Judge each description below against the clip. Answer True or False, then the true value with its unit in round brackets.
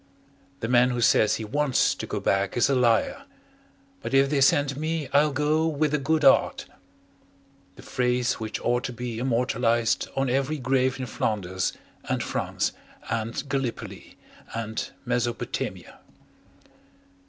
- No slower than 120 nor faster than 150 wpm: True (140 wpm)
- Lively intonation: False (3.3 semitones)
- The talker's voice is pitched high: False (125 Hz)